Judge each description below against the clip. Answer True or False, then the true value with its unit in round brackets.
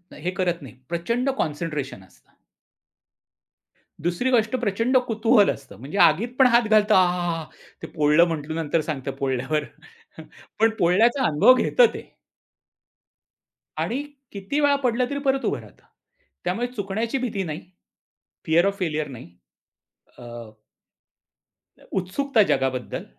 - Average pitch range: False (7.2 semitones)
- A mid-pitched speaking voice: True (180 Hz)